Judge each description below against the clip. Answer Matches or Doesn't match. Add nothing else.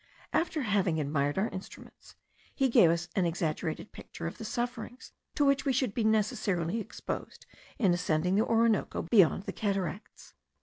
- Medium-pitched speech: Doesn't match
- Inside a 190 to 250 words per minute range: Doesn't match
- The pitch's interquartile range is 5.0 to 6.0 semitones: Matches